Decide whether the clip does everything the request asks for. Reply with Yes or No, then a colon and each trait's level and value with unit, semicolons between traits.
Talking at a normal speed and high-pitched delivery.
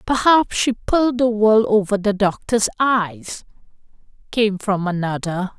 No: slow, 130 wpm; high, 210 Hz